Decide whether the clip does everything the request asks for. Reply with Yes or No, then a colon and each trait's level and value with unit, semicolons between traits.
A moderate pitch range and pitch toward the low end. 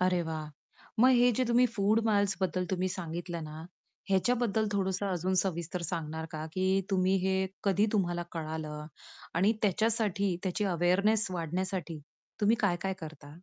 No: average, 3.2 semitones; medium, 185 Hz